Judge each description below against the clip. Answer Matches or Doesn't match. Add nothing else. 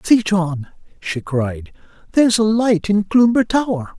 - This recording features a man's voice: Matches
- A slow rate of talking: Doesn't match